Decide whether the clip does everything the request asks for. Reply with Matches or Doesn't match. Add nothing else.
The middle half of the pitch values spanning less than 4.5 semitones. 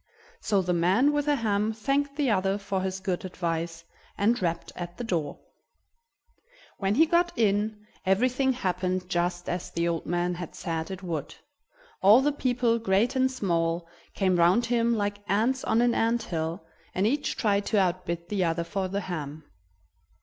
Doesn't match